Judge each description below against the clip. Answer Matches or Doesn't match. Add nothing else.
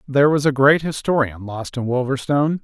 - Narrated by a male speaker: Matches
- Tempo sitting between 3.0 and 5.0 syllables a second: Doesn't match